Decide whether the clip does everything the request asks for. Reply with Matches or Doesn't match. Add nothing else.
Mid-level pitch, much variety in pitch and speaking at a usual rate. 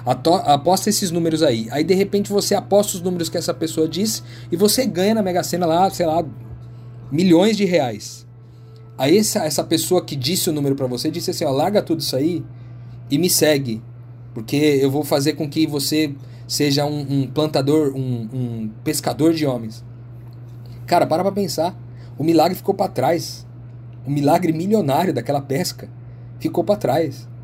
Matches